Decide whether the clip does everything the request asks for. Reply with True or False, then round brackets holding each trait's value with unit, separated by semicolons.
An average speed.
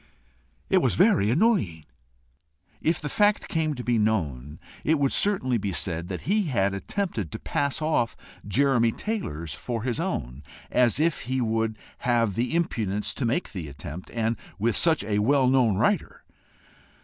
True (160 wpm)